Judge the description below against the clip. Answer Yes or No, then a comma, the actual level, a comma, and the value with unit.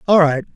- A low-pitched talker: No, medium, 165 Hz